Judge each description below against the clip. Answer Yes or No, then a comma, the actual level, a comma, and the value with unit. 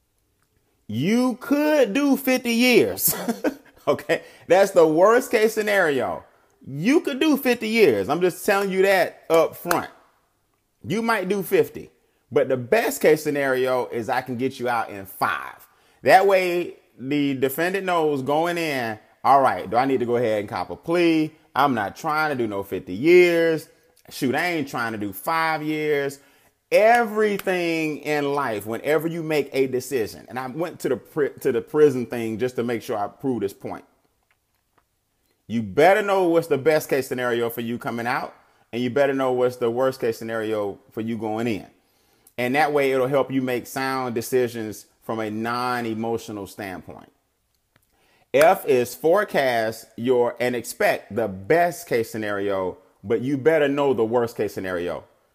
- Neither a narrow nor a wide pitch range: No, wide, 6.7 semitones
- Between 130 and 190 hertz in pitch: Yes, medium, 140 Hz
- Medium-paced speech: Yes, average, 170 wpm